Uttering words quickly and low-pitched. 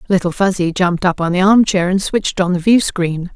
No: fast, 215 wpm; medium, 185 Hz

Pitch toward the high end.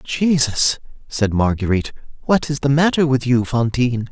No: low, 130 Hz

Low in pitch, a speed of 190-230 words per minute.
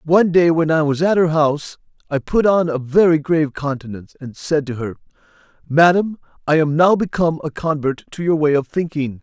No: medium, 155 Hz; average, 200 wpm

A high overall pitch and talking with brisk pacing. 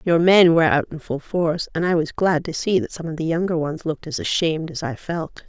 No: medium, 165 Hz; fast, 275 wpm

